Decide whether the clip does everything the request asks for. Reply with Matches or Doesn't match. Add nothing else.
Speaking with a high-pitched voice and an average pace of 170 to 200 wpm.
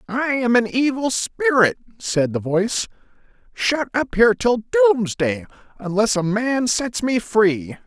Doesn't match